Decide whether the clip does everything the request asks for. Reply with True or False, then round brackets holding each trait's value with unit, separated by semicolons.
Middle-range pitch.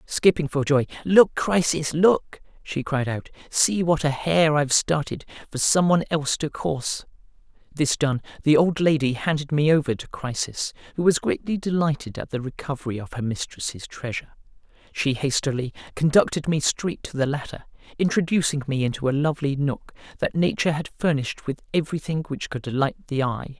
True (145 Hz)